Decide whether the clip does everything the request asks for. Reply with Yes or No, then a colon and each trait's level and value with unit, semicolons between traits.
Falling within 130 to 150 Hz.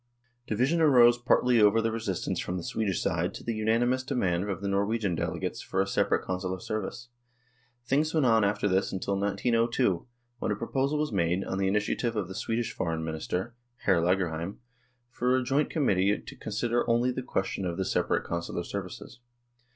No: low, 105 Hz